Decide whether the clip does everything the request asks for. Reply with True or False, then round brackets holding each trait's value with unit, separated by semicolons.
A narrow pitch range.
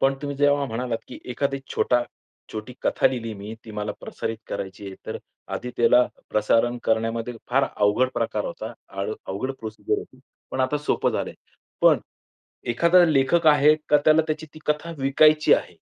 False (4.5 semitones)